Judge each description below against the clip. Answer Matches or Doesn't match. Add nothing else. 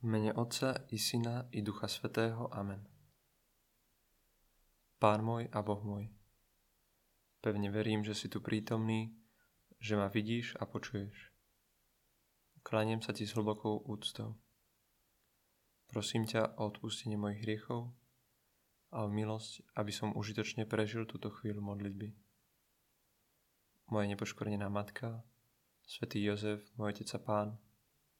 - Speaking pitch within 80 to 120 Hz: Matches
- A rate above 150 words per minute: Doesn't match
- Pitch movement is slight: Matches